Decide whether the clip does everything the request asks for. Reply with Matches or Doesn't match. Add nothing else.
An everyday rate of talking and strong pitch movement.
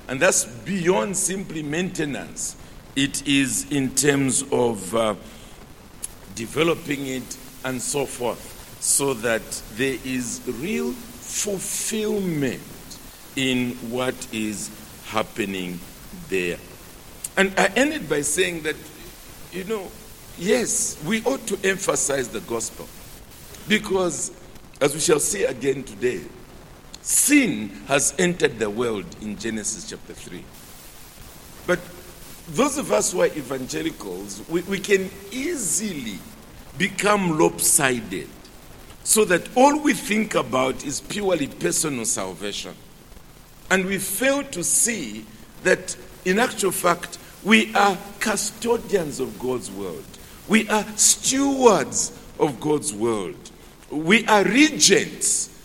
Doesn't match